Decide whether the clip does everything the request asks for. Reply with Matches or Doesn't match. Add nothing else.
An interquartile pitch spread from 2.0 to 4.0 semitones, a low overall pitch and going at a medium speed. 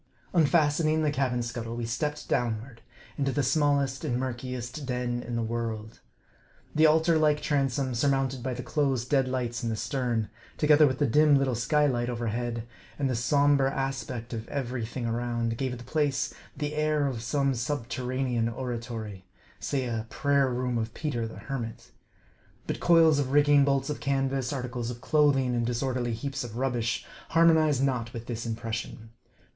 Matches